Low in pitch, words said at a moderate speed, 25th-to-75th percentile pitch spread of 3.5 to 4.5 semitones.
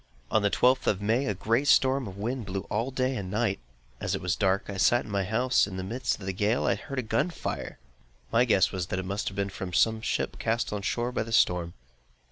No: low, 105 Hz; fast, 260 wpm; average, 3.9 semitones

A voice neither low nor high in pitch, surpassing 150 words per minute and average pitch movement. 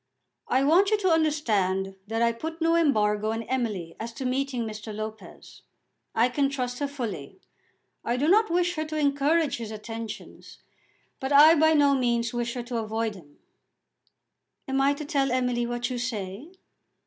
No: very high, 250 Hz; average, 170 wpm; average, 4.5 semitones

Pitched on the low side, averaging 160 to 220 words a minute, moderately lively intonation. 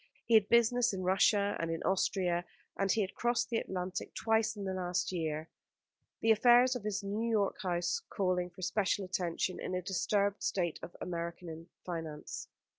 No: high, 190 Hz; average, 175 wpm; average, 3.6 semitones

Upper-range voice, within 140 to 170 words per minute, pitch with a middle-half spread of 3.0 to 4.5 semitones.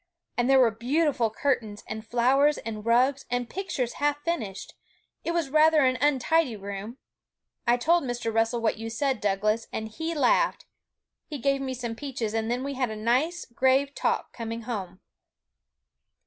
Yes: high, 245 Hz; average, 165 wpm; average, 4.0 semitones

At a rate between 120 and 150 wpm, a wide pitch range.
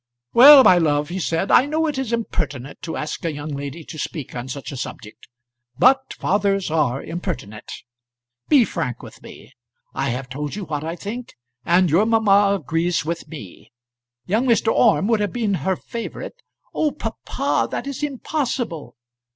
No: average, 175 wpm; wide, 7.8 semitones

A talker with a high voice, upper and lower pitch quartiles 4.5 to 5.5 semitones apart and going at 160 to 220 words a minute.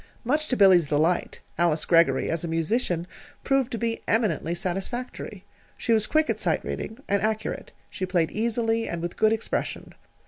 Yes: high, 200 Hz; average, 5.1 semitones; average, 170 wpm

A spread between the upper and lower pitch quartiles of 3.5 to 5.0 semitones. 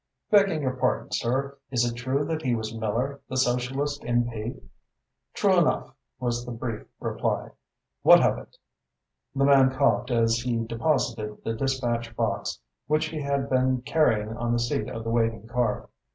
No: average, 2.9 semitones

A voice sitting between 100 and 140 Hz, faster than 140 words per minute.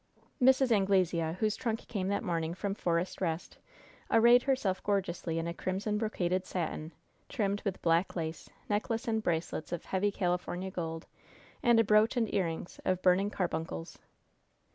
No: high, 190 Hz; average, 150 wpm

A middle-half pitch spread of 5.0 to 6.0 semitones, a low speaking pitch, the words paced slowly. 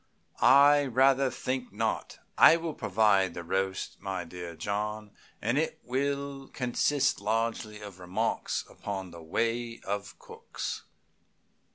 Yes: wide, 5.5 semitones; low, 110 Hz; slow, 125 wpm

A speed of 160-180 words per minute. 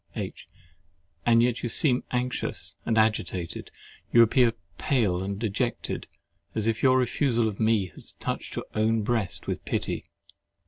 No: average, 145 wpm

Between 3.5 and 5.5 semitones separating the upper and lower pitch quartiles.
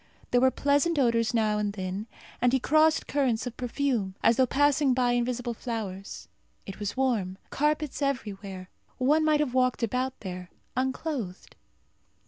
Yes: average, 4.7 semitones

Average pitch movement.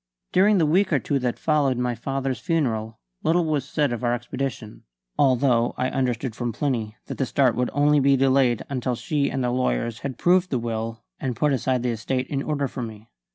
Yes: average, 3.1 semitones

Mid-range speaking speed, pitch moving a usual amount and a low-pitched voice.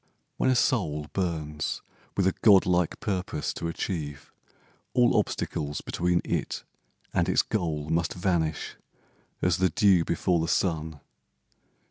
No: slow, 130 wpm; average, 3.3 semitones; very low, 85 Hz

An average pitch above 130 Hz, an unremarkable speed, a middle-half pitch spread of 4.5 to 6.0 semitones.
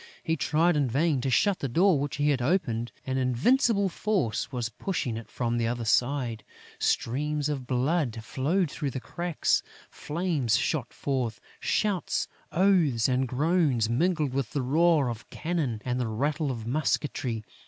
Yes: medium, 140 Hz; average, 160 wpm; average, 5.3 semitones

